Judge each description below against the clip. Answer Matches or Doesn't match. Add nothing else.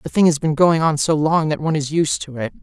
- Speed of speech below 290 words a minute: Doesn't match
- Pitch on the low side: Doesn't match